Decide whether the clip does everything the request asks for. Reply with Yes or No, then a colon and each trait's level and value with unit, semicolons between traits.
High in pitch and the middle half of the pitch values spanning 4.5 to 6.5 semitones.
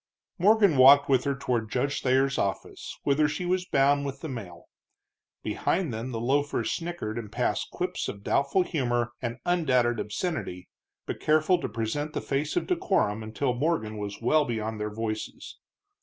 No: low, 135 Hz; average, 5.3 semitones